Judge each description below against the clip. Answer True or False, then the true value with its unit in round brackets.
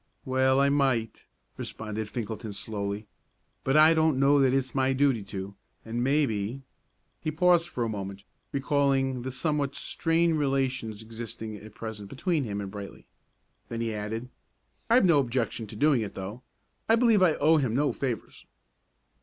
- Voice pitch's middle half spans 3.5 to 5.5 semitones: True (4.6 semitones)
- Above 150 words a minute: True (160 wpm)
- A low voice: True (130 Hz)